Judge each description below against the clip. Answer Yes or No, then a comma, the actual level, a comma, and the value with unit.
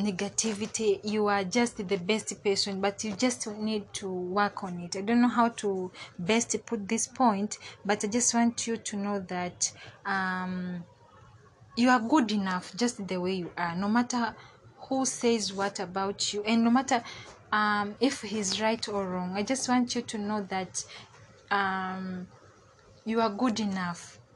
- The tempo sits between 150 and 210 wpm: Yes, average, 170 wpm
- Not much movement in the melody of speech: No, average, 3.4 semitones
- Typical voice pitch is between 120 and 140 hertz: No, high, 205 Hz